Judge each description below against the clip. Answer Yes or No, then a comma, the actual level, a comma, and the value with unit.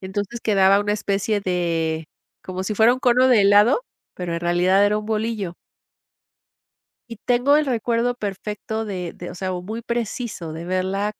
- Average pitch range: Yes, average, 3.7 semitones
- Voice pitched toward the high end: Yes, high, 205 Hz